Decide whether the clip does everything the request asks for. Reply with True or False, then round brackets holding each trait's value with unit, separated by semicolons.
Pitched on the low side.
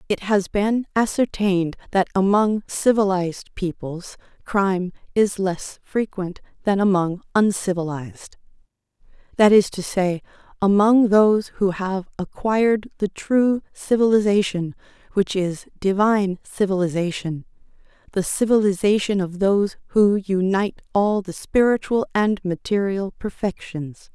False (195 Hz)